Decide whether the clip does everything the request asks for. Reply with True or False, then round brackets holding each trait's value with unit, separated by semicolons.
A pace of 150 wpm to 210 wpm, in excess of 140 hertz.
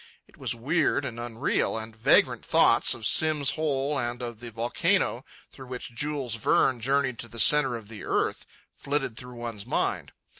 False (175 wpm; 120 Hz)